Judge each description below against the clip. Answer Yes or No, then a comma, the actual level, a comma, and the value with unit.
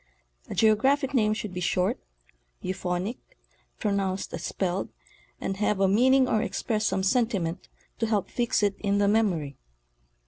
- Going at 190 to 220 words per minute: No, average, 150 wpm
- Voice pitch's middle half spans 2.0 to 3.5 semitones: Yes, average, 3.0 semitones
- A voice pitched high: Yes, high, 205 Hz